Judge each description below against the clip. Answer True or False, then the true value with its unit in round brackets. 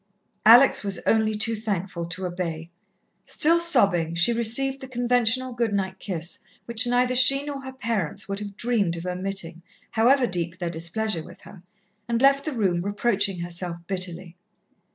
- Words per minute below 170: True (160 wpm)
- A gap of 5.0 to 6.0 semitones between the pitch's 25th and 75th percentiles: True (5.5 semitones)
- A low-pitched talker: False (205 Hz)